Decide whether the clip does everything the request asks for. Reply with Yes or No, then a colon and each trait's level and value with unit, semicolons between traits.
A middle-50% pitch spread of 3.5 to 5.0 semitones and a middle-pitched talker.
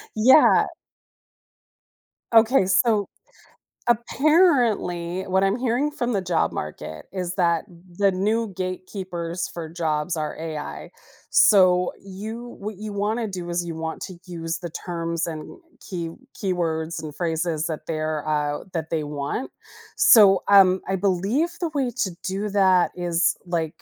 Yes: average, 3.9 semitones; medium, 180 Hz